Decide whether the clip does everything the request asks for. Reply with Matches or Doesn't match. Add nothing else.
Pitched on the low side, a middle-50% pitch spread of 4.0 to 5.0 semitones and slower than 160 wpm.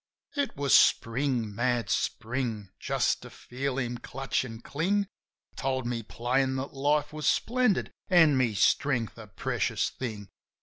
Doesn't match